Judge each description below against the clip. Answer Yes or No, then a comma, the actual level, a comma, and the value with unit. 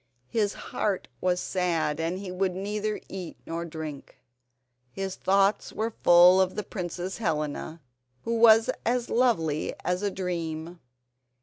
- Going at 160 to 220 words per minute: No, slow, 135 wpm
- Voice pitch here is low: No, medium, 185 Hz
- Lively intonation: No, average, 3.7 semitones